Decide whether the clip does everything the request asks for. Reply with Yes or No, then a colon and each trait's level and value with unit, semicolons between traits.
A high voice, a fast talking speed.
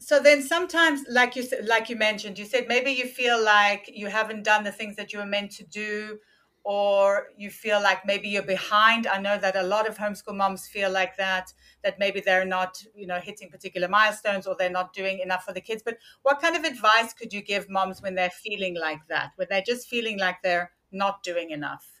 Yes: high, 205 Hz; fast, 225 wpm